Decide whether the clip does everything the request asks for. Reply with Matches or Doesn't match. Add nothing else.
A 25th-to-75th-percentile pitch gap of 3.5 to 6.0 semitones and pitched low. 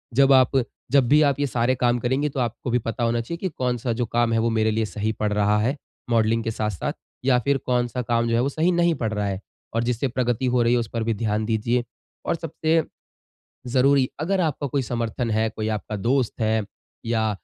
Doesn't match